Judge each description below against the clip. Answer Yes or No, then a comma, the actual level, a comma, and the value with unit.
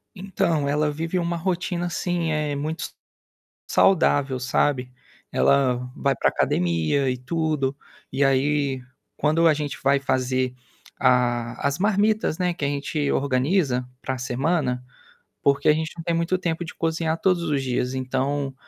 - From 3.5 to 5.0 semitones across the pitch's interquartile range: Yes, average, 4.0 semitones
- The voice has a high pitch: No, medium, 145 Hz